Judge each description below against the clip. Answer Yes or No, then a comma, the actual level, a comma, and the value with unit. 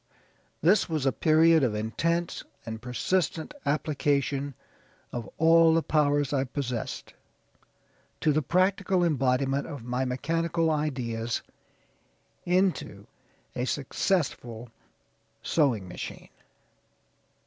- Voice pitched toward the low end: No, medium, 145 Hz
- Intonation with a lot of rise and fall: No, average, 4.6 semitones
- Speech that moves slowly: Yes, slow, 95 wpm